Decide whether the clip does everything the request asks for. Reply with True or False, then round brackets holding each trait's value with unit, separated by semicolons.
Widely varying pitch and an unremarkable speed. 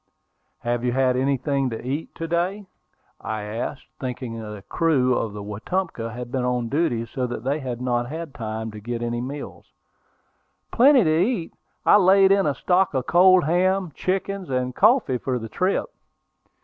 True (6.7 semitones; 175 wpm)